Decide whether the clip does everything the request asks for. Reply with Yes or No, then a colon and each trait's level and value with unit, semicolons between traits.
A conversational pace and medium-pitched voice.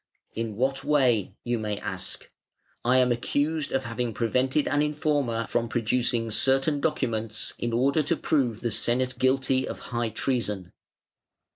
No: average, 145 wpm; low, 125 Hz